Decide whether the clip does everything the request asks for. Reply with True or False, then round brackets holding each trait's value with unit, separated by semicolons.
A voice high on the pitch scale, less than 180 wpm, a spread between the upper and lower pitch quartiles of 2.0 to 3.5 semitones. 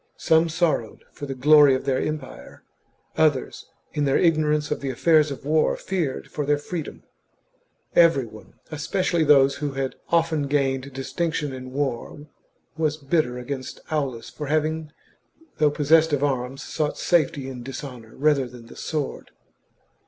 False (145 Hz; 155 wpm; 2.6 semitones)